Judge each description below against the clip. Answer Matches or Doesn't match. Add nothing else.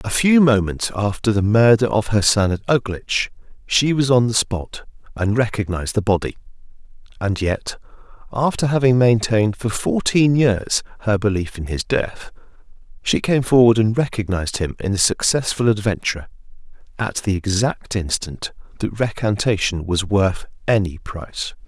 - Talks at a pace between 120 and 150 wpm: Matches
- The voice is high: Doesn't match